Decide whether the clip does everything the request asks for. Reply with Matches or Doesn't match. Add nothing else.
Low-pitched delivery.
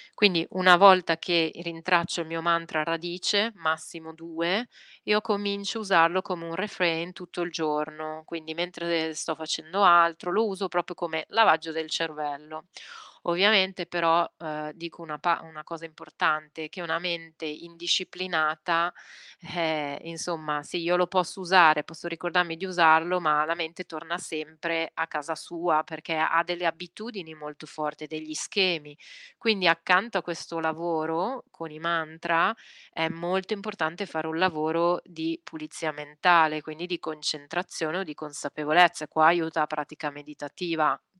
Doesn't match